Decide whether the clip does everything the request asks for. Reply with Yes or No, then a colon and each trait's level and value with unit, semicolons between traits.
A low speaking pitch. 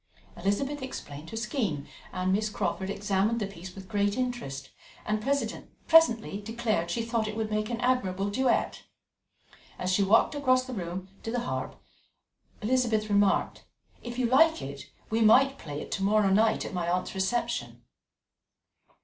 No: high, 215 Hz